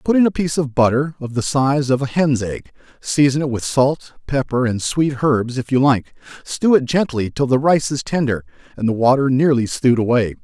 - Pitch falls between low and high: No, low, 130 Hz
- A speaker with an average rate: No, fast, 220 wpm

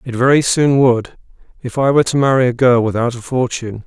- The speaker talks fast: Yes, fast, 215 wpm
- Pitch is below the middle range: Yes, low, 125 Hz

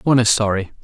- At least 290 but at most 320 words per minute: No, fast, 215 wpm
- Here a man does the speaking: Yes, male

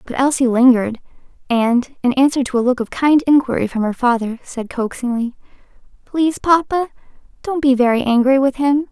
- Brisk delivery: No, average, 170 wpm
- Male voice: No, female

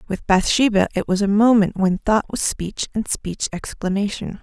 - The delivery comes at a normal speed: Yes, average, 175 wpm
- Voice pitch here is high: Yes, high, 200 Hz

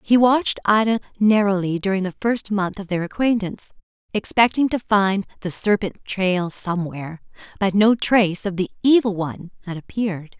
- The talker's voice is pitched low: No, high, 200 Hz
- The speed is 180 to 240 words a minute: No, average, 155 wpm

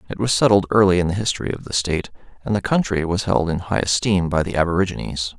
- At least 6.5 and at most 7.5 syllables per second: Yes, 6.7 syllables/s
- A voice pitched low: Yes, very low, 90 Hz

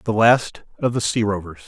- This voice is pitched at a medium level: No, low, 110 Hz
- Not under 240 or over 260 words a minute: No, fast, 215 wpm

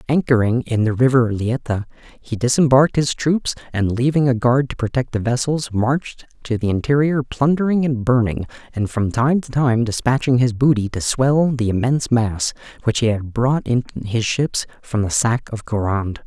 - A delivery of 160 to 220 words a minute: Yes, average, 180 wpm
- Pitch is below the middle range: Yes, low, 125 Hz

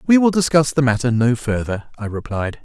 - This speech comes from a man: Yes, male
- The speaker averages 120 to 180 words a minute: No, fast, 205 wpm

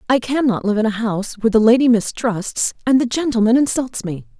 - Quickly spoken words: Yes, fast, 220 wpm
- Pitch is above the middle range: Yes, high, 230 Hz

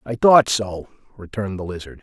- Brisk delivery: No, average, 180 wpm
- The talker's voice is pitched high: No, low, 105 Hz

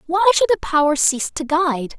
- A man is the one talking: No, female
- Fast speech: Yes, fast, 210 wpm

